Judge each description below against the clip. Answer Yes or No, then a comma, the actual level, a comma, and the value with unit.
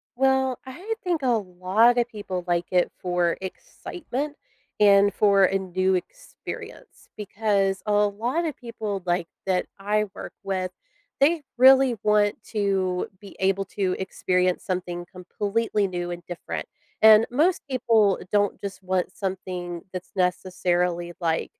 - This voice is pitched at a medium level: No, high, 195 Hz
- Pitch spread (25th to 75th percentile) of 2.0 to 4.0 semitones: Yes, average, 3.7 semitones